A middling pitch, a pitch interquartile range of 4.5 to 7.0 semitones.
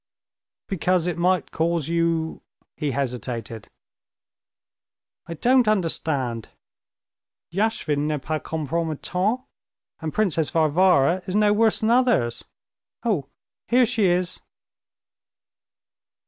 Yes: medium, 170 Hz; wide, 5.4 semitones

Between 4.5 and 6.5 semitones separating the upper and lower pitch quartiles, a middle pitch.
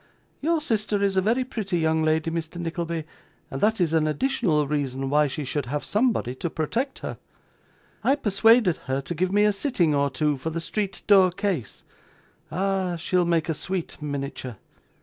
Yes: average, 5.2 semitones; medium, 170 Hz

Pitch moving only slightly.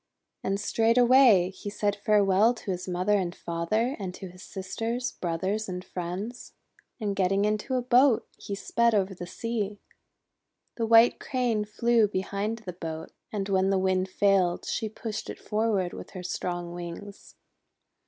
No: average, 3.4 semitones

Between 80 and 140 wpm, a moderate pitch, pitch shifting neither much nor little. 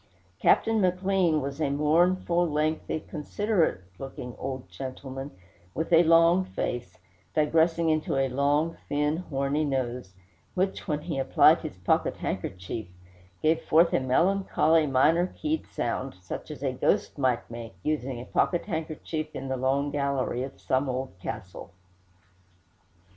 Yes: slow, 135 wpm; medium, 150 Hz; average, 4.0 semitones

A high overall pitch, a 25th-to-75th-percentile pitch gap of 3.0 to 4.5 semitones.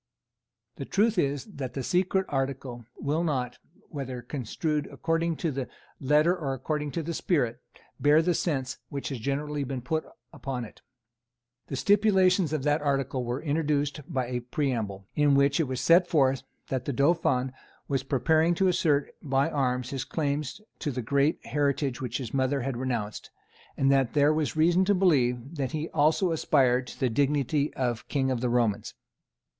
No: medium, 140 Hz; average, 3.3 semitones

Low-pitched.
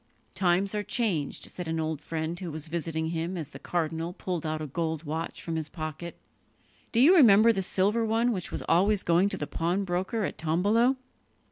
No: medium, 175 Hz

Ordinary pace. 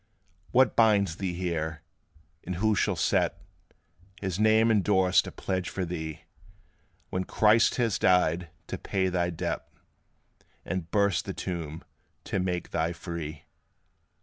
No: slow, 130 wpm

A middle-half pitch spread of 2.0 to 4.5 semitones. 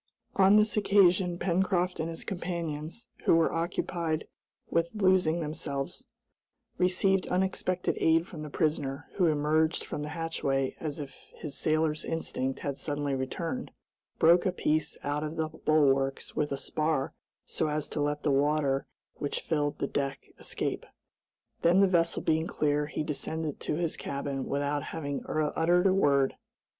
Yes: average, 3.0 semitones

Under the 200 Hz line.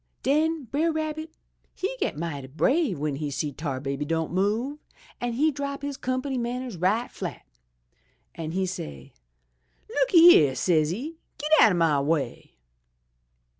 No: high, 215 Hz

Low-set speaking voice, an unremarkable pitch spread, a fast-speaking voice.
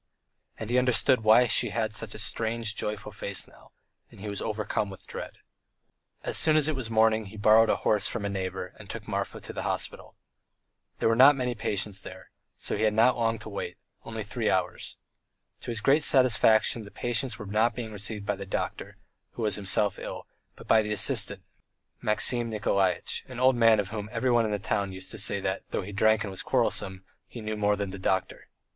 No: low, 110 Hz; narrow, 2.3 semitones; fast, 215 wpm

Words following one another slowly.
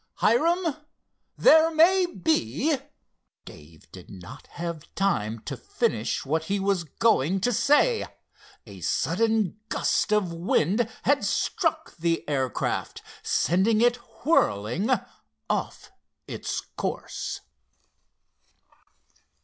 Yes: slow, 100 wpm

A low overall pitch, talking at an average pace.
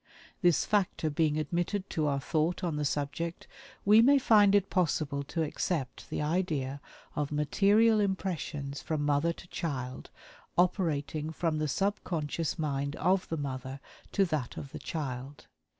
No: medium, 155 Hz; average, 150 wpm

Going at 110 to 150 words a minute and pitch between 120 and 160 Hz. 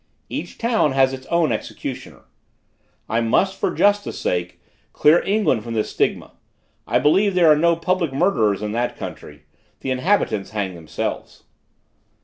Yes: average, 145 wpm; low, 135 Hz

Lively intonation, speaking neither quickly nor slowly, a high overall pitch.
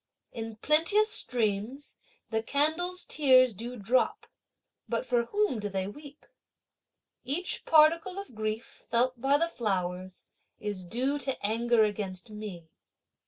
No: wide, 5.7 semitones; slow, 125 wpm; high, 240 Hz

